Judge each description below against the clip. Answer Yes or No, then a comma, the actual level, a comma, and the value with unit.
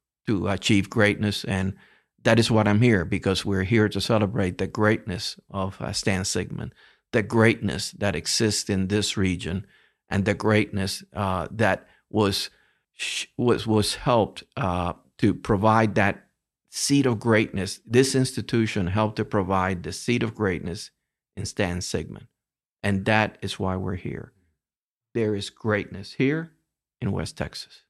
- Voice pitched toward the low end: Yes, low, 105 Hz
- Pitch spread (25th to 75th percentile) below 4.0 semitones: Yes, narrow, 2.6 semitones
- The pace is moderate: Yes, average, 150 wpm